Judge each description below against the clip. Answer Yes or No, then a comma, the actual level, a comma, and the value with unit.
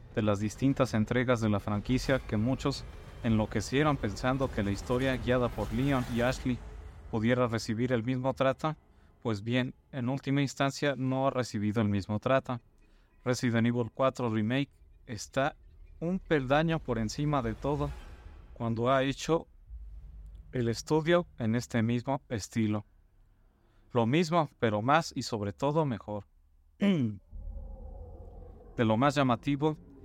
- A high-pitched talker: No, low, 120 Hz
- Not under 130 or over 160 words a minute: Yes, average, 135 wpm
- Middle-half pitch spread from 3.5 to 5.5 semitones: Yes, average, 4.3 semitones